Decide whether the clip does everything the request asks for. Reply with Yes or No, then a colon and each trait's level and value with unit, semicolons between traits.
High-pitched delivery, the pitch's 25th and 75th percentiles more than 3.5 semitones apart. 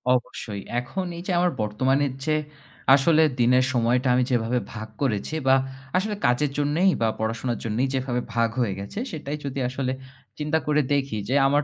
No: low, 130 Hz; average, 4.0 semitones